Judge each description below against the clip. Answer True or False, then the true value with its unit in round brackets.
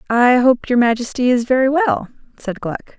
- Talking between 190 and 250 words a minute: False (180 wpm)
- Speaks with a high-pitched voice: True (250 Hz)